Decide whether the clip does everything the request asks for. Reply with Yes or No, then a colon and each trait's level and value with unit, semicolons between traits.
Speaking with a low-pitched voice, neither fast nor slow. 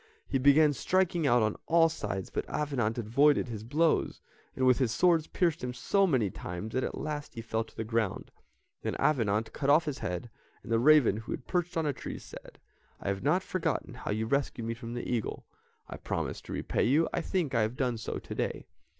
No: low, 130 Hz; fast, 220 wpm